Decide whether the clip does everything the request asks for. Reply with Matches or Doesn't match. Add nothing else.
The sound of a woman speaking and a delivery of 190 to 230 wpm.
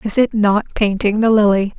Matches